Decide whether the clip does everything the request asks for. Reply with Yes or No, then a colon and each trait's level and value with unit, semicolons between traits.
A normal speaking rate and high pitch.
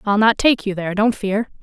No: fast, 260 wpm; high, 210 Hz